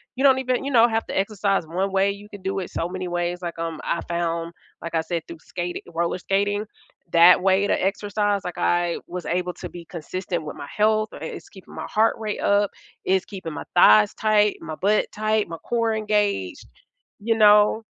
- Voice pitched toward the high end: Yes, high, 195 Hz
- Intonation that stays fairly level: No, average, 3.3 semitones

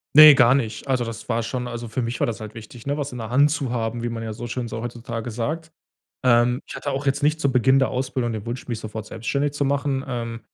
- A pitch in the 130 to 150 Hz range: No, low, 120 Hz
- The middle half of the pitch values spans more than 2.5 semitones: Yes, average, 2.9 semitones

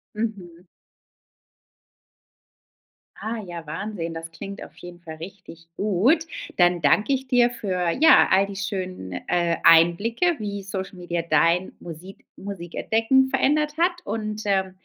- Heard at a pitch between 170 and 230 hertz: Yes, high, 190 Hz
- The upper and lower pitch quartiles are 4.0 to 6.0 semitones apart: Yes, average, 4.5 semitones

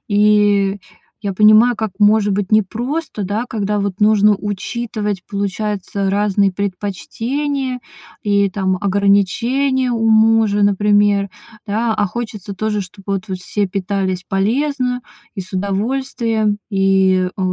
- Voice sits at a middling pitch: No, high, 205 Hz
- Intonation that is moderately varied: No, narrow, 2.1 semitones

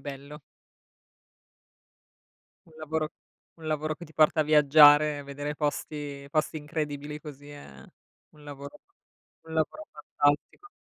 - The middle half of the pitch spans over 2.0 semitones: No, narrow, 1.3 semitones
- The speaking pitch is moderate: Yes, medium, 150 Hz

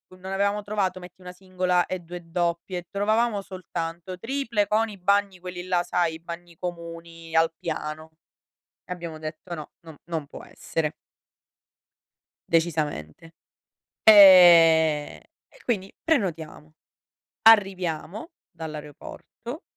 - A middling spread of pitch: Yes, average, 3.1 semitones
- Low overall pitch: No, medium, 175 Hz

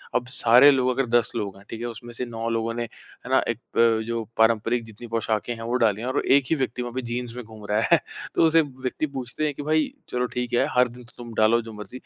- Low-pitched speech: Yes, low, 120 Hz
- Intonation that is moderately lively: No, narrow, 2.0 semitones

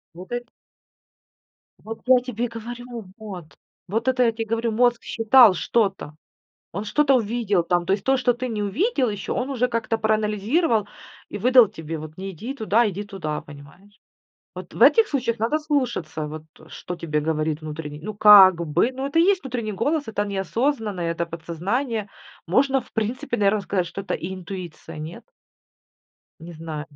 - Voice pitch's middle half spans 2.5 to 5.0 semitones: No, wide, 5.4 semitones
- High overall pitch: Yes, high, 215 Hz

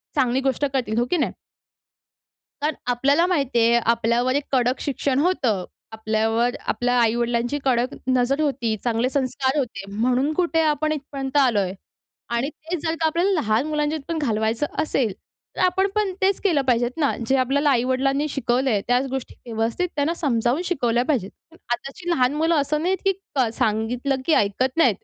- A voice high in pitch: Yes, very high, 265 Hz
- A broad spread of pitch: No, average, 4.1 semitones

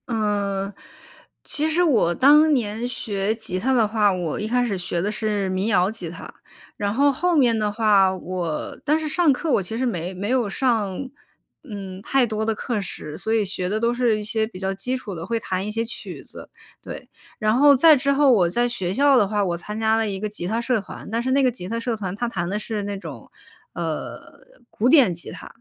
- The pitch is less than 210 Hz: No, high, 215 Hz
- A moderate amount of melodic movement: Yes, average, 4.2 semitones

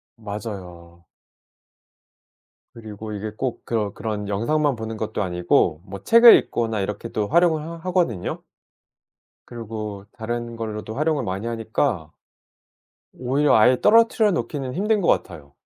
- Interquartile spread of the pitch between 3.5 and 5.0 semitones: No, wide, 5.6 semitones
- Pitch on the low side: Yes, low, 115 Hz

